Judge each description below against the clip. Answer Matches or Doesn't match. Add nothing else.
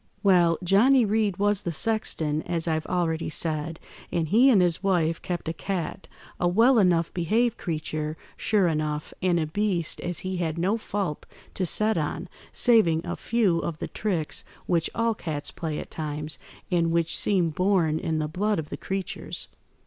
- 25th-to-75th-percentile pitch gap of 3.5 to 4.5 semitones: Matches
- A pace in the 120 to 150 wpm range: Doesn't match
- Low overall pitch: Doesn't match